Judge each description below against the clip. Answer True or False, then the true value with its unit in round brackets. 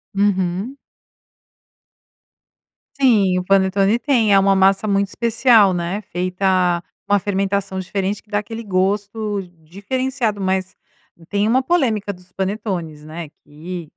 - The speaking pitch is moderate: False (195 Hz)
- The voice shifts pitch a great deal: False (2.4 semitones)